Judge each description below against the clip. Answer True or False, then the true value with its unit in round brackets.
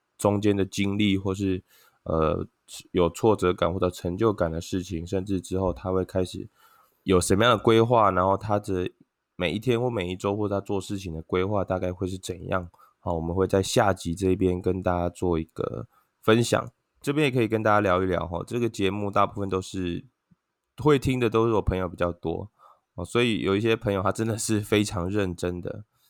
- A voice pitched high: False (95 Hz)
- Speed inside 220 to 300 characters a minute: True (290 characters per minute)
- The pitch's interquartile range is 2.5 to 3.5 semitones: True (2.8 semitones)